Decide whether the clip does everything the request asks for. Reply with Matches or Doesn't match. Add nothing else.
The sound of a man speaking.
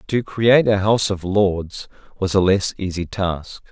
Matches